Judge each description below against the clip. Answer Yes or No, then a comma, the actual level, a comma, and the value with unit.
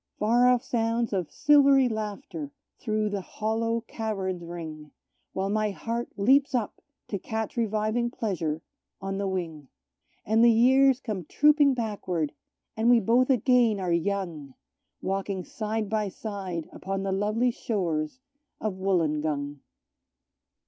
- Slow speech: Yes, slow, 130 wpm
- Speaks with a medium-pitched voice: No, high, 215 Hz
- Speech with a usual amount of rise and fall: Yes, average, 4.0 semitones